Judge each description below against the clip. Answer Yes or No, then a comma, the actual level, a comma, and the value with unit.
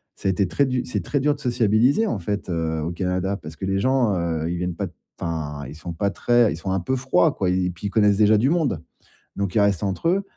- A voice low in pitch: Yes, low, 100 Hz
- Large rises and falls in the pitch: Yes, wide, 5.7 semitones